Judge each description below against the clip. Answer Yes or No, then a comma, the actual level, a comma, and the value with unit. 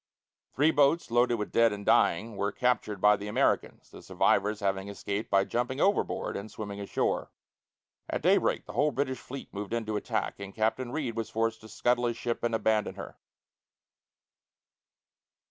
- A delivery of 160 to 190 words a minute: Yes, average, 170 wpm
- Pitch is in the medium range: No, low, 115 Hz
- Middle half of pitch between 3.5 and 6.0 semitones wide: No, average, 3.1 semitones